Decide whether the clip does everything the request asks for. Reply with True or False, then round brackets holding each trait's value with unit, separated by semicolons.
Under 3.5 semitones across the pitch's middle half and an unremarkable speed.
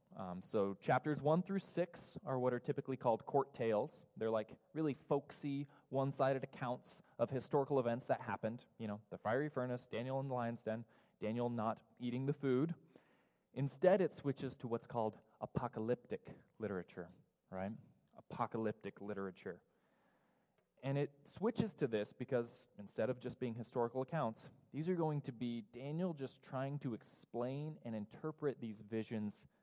False (4.0 semitones; 155 wpm)